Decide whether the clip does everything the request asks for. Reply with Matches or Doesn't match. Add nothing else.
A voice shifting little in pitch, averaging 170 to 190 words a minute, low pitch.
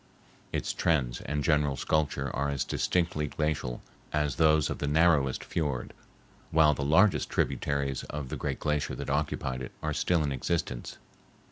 Doesn't match